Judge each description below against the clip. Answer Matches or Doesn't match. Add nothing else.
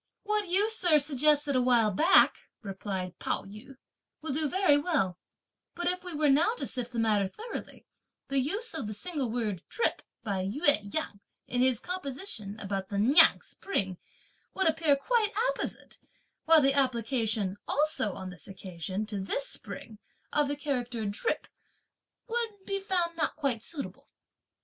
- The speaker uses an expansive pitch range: Matches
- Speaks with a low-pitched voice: Doesn't match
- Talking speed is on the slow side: Doesn't match